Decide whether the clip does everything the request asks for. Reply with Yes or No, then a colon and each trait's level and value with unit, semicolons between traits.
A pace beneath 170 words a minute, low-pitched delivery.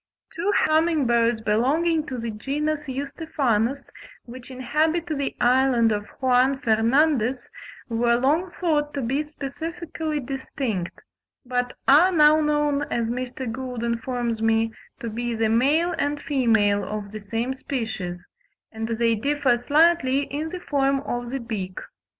No: average, 140 wpm; very high, 260 Hz